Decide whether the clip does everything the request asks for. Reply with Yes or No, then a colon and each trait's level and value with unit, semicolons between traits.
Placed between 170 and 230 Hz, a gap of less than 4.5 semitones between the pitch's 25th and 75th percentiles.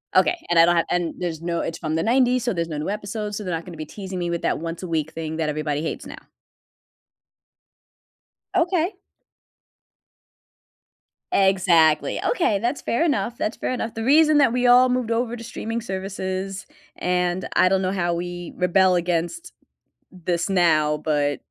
No: medium, 185 Hz; wide, 5.5 semitones